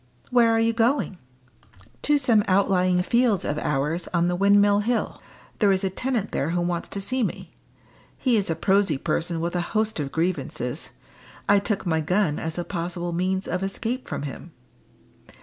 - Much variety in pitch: No, average, 4.0 semitones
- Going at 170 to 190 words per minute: Yes, average, 180 wpm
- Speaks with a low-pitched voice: No, high, 190 Hz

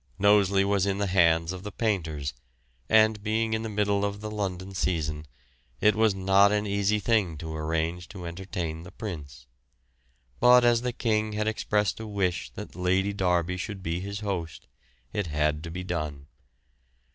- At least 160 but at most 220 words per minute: Yes, average, 170 wpm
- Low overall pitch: Yes, very low, 95 Hz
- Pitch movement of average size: Yes, average, 3.8 semitones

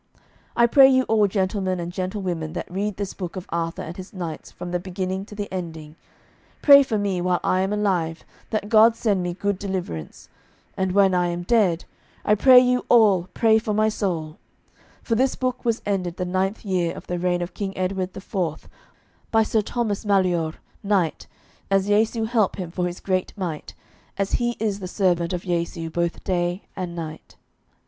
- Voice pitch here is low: No, high, 190 Hz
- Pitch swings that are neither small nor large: Yes, average, 3.0 semitones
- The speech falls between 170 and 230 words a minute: Yes, average, 190 wpm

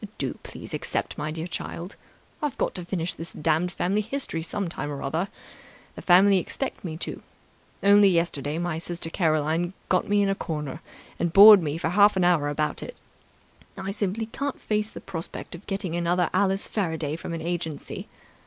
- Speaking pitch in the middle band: Yes, medium, 175 Hz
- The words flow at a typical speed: Yes, average, 180 wpm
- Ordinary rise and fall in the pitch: Yes, average, 3.4 semitones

